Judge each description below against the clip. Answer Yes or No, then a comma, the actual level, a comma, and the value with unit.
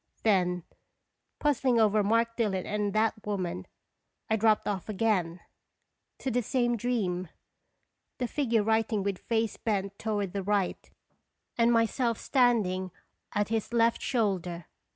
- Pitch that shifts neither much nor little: Yes, average, 3.0 semitones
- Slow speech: Yes, slow, 130 wpm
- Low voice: No, high, 215 Hz